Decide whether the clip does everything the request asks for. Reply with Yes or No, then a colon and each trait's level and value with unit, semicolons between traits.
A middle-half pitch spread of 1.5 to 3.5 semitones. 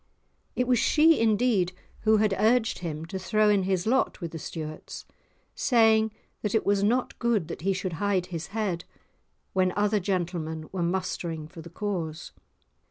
No: average, 4.2 semitones